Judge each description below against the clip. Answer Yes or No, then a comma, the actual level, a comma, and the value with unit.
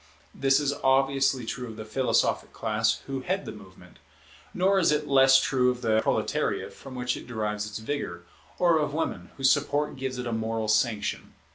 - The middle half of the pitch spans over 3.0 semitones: Yes, average, 3.9 semitones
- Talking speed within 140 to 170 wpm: No, average, 185 wpm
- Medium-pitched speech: No, low, 130 Hz